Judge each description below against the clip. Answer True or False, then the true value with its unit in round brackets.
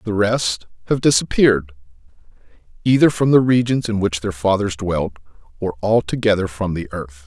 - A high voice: False (100 Hz)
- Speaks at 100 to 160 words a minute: True (150 wpm)